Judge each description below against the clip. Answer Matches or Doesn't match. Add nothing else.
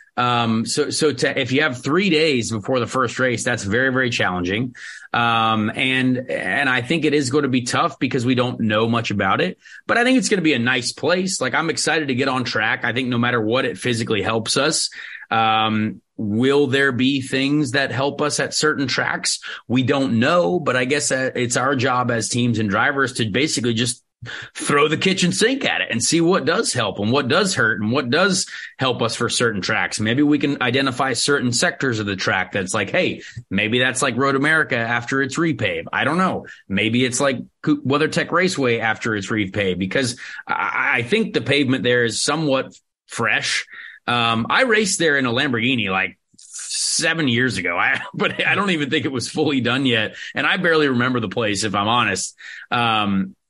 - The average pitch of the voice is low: Matches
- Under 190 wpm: Doesn't match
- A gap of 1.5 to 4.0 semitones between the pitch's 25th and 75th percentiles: Matches